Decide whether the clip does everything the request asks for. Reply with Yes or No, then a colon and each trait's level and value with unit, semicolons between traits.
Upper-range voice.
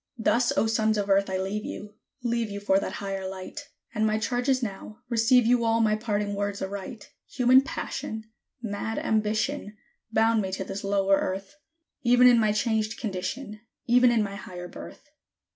Yes: high, 215 Hz